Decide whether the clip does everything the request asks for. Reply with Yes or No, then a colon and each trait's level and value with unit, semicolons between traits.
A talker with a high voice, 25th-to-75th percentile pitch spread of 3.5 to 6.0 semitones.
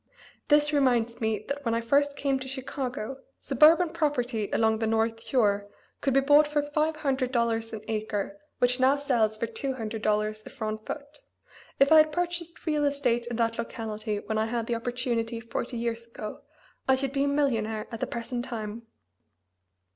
Yes: high, 240 Hz; average, 4.0 semitones